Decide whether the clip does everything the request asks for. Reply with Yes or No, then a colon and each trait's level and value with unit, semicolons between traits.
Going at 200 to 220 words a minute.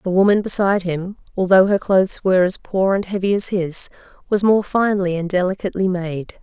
No: average, 185 wpm